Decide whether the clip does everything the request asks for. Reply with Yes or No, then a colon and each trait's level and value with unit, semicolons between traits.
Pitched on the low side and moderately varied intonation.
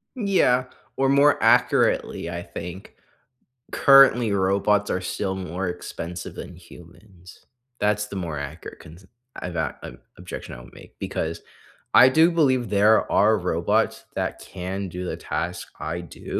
Yes: very low, 95 Hz; average, 4.1 semitones